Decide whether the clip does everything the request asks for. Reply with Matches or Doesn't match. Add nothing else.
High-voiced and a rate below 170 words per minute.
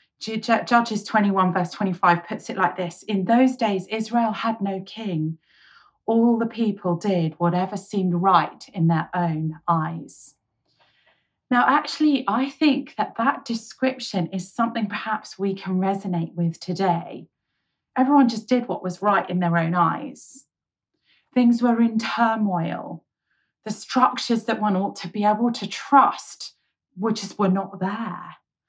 Matches